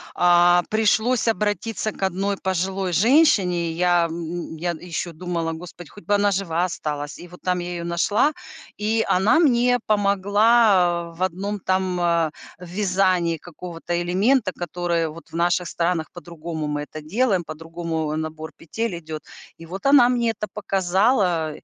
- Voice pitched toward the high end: No, medium, 180 Hz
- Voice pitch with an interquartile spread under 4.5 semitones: Yes, average, 3.4 semitones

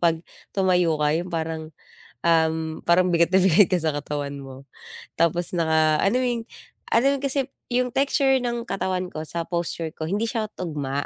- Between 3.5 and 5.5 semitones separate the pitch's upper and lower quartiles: Yes, average, 4.5 semitones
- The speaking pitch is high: No, medium, 170 Hz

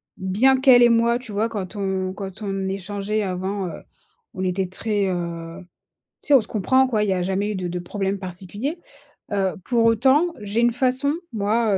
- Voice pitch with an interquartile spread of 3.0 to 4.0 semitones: Yes, average, 3.7 semitones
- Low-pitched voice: No, high, 205 Hz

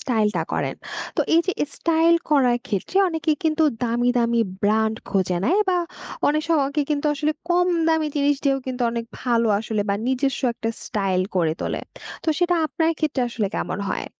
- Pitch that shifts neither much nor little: No, wide, 6.3 semitones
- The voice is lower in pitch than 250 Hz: No, very high, 260 Hz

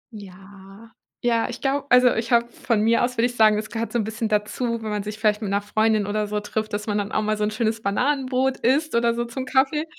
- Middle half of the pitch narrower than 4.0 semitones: Yes, narrow, 2.5 semitones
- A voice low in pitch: No, high, 225 Hz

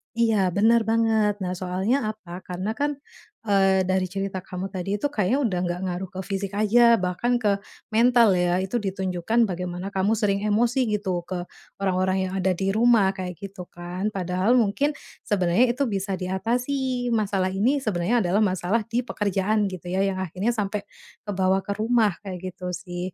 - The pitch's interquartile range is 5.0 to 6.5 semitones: No, average, 3.2 semitones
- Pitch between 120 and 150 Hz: No, high, 195 Hz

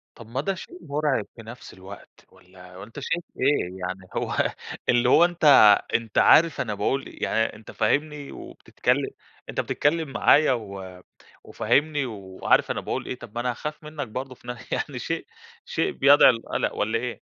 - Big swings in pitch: Yes, wide, 6.0 semitones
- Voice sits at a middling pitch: No, low, 120 Hz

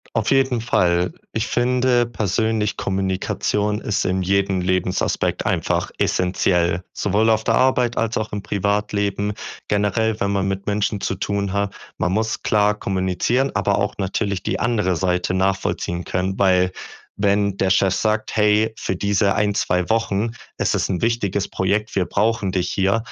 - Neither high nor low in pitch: No, low, 100 Hz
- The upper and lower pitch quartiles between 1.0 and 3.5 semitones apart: Yes, narrow, 2.6 semitones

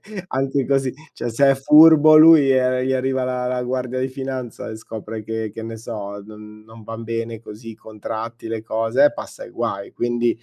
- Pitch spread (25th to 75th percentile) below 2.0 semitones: No, average, 2.9 semitones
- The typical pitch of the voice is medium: No, low, 120 Hz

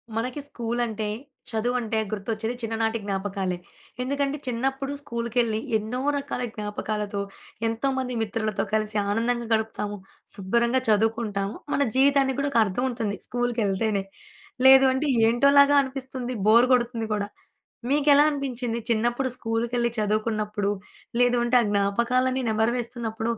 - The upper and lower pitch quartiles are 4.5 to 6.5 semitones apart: No, average, 2.9 semitones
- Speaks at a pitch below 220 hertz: No, high, 235 Hz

